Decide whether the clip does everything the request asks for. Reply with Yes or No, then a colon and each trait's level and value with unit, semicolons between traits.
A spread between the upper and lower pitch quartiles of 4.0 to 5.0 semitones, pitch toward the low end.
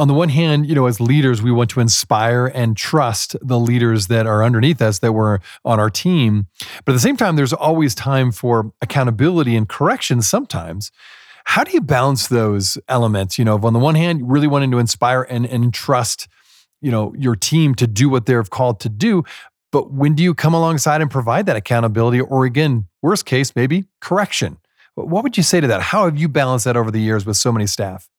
Yes: average, 4.5 semitones; low, 125 Hz